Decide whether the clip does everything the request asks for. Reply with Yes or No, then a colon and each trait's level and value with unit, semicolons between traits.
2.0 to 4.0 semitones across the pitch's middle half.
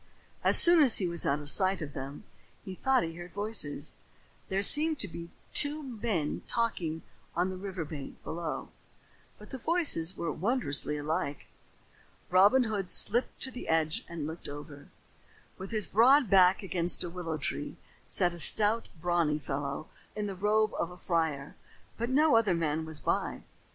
No: wide, 5.4 semitones